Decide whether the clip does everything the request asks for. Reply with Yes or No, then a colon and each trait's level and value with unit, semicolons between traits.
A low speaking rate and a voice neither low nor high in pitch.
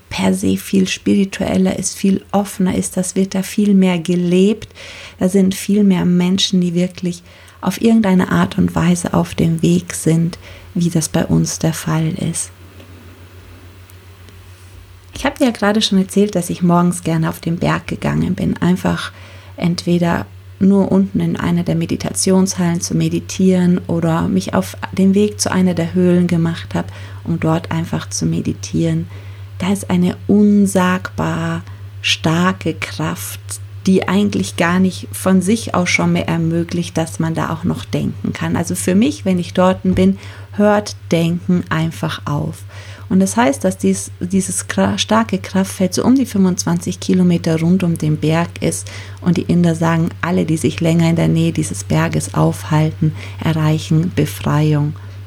No: average, 160 wpm; medium, 165 Hz